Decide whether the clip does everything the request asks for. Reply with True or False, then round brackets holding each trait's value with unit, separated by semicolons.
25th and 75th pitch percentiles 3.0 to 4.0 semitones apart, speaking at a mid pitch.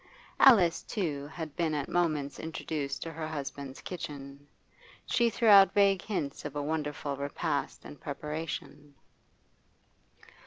True (3.3 semitones; 150 Hz)